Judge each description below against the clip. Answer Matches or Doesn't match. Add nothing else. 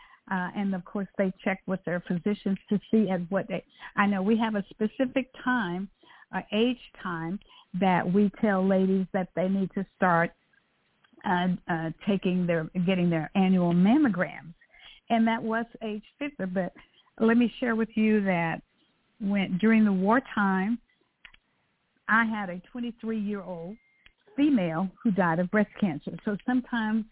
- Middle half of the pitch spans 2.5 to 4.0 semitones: Matches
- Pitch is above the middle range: Matches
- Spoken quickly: Doesn't match